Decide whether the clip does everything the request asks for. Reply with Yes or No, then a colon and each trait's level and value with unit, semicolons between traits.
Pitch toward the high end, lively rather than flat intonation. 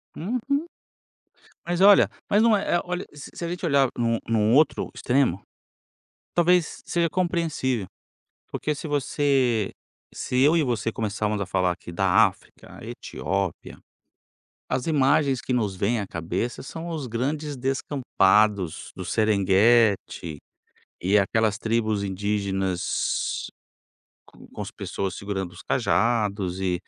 No: low, 115 Hz; wide, 6.9 semitones